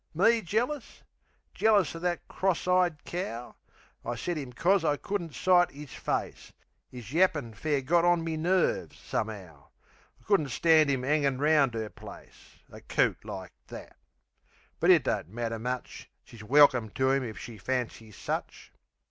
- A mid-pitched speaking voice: Yes, medium, 150 Hz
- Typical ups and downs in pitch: No, wide, 6.3 semitones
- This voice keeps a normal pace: Yes, average, 155 wpm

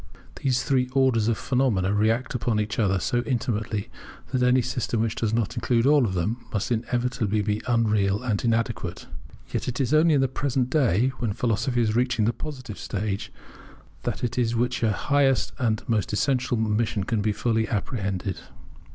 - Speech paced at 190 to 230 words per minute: No, average, 175 wpm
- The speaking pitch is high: No, low, 115 Hz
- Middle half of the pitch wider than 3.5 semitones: No, average, 2.9 semitones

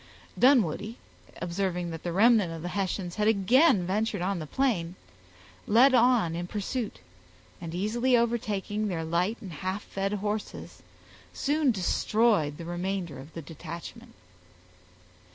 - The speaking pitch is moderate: No, high, 195 Hz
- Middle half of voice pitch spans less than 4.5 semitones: No, average, 4.9 semitones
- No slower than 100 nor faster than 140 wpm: Yes, slow, 135 wpm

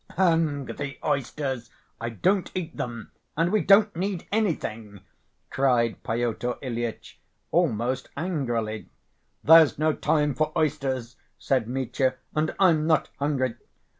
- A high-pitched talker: No, medium, 140 Hz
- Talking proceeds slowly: Yes, slow, 120 wpm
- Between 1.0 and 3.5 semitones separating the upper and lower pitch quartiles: No, average, 5.1 semitones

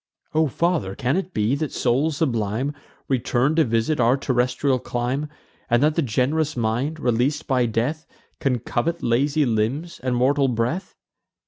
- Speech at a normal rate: Yes, average, 150 wpm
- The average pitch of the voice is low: Yes, low, 130 Hz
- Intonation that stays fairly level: No, average, 4.0 semitones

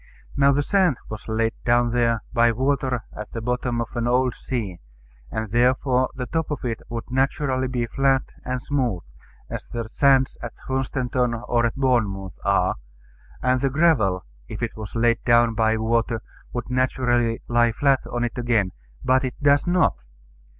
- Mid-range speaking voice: No, low, 120 Hz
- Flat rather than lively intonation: Yes, narrow, 2.3 semitones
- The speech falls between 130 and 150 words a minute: No, average, 170 wpm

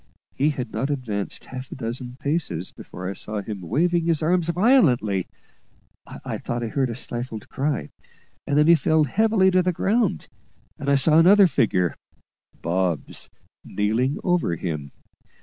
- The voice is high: No, low, 135 Hz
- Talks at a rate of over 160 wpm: No, average, 155 wpm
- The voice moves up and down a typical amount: No, wide, 7.9 semitones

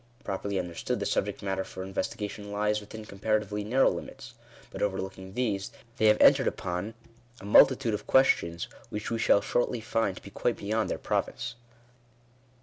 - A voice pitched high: No, low, 105 Hz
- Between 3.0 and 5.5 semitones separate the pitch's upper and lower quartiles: No, narrow, 2.4 semitones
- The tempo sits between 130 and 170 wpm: Yes, average, 165 wpm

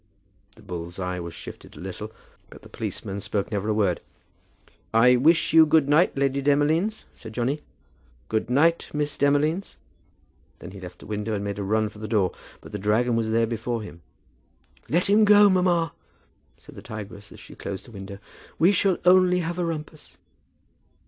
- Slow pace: No, average, 180 wpm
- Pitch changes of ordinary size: No, wide, 7.8 semitones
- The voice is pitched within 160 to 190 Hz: No, low, 120 Hz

